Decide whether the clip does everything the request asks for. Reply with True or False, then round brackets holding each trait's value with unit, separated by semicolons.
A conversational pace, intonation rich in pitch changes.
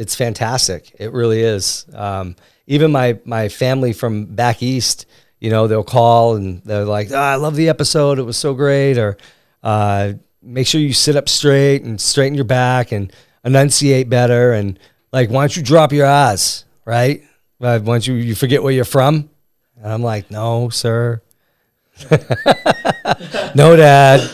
False (170 wpm; 3.8 semitones)